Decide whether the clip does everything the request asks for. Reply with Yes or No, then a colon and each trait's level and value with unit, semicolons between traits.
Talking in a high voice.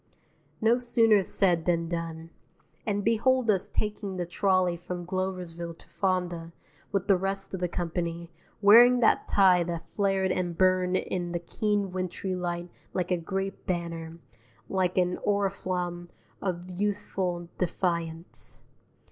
No: medium, 180 Hz